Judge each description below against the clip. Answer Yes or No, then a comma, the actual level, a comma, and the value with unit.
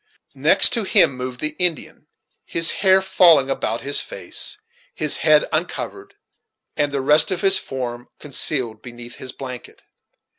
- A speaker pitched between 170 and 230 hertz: No, medium, 140 Hz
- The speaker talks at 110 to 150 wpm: Yes, average, 145 wpm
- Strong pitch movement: Yes, wide, 6.1 semitones